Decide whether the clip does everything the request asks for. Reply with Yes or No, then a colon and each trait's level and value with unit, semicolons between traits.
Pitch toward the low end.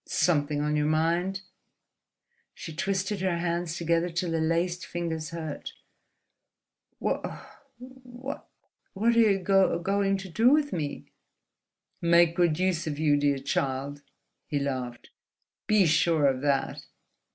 No: medium, 170 Hz